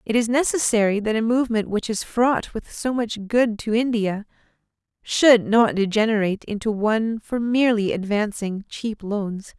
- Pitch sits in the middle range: No, high, 220 Hz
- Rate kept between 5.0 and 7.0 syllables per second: No, 4.7 syllables/s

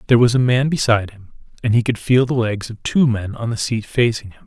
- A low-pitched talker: Yes, low, 115 Hz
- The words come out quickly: Yes, fast, 270 wpm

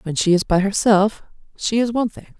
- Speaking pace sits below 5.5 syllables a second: No, 5.7 syllables/s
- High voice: Yes, high, 205 Hz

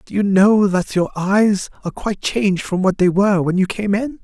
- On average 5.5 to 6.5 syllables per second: No, 5.3 syllables/s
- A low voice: No, high, 195 Hz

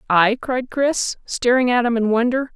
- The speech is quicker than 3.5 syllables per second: Yes, 4.5 syllables/s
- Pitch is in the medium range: No, high, 240 Hz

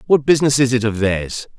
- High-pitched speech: No, low, 120 Hz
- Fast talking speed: Yes, fast, 230 wpm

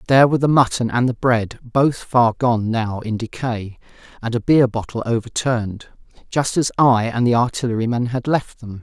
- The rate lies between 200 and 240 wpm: No, average, 185 wpm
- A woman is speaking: No, male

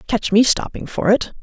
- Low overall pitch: No, high, 215 Hz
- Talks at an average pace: No, fast, 210 wpm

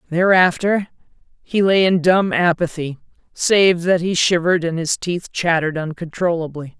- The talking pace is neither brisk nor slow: No, slow, 130 wpm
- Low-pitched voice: No, medium, 175 Hz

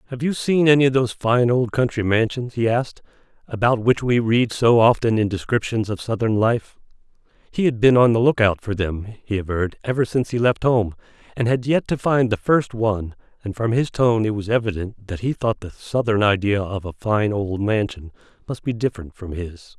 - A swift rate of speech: Yes, fast, 210 wpm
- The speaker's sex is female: No, male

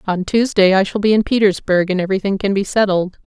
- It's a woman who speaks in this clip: Yes, female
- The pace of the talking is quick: Yes, fast, 220 wpm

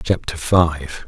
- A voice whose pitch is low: Yes, very low, 80 Hz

